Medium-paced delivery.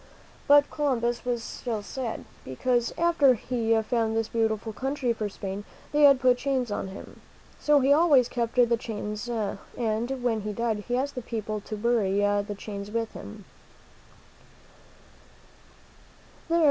Yes: average, 145 wpm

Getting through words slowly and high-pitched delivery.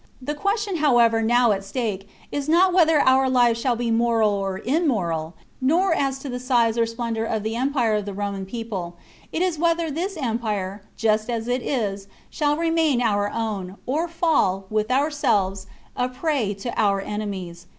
No: average, 175 wpm; high, 235 Hz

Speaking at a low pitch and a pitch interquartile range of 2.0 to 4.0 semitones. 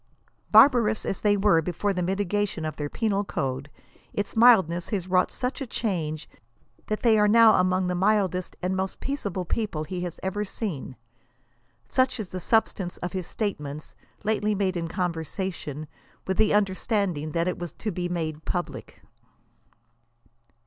No: high, 190 Hz; average, 3.4 semitones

